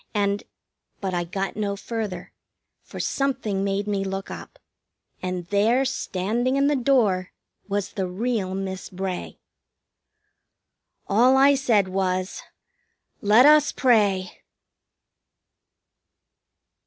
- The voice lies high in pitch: Yes, high, 200 Hz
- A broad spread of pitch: No, average, 4.3 semitones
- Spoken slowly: Yes, slow, 110 wpm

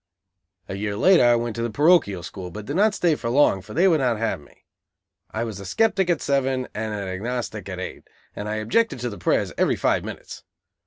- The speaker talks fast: Yes, fast, 220 wpm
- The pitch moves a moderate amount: No, wide, 6.1 semitones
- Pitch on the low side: Yes, low, 115 Hz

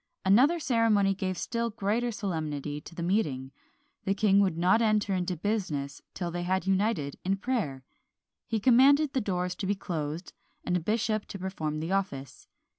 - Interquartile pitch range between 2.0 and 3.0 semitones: No, average, 4.5 semitones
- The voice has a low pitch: No, high, 195 Hz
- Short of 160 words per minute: No, average, 170 wpm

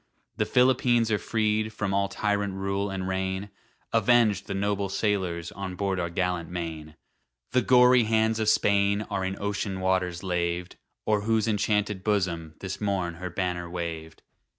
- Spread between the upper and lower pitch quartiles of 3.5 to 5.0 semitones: No, average, 2.7 semitones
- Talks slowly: No, average, 155 wpm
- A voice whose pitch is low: Yes, low, 100 Hz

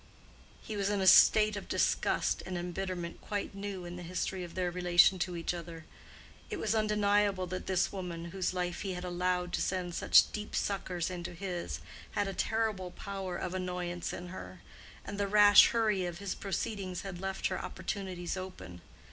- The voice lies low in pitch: No, medium, 185 Hz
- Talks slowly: No, average, 180 wpm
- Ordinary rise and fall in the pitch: No, narrow, 2.1 semitones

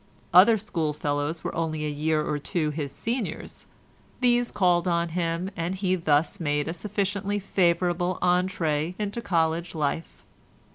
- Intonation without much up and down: No, average, 3.4 semitones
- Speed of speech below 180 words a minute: Yes, average, 140 wpm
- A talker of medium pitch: Yes, medium, 170 Hz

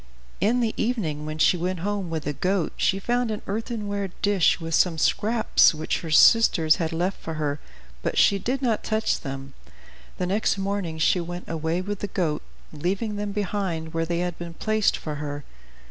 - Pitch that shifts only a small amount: No, average, 4.3 semitones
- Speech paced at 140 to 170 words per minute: No, average, 190 wpm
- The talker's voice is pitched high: No, medium, 180 Hz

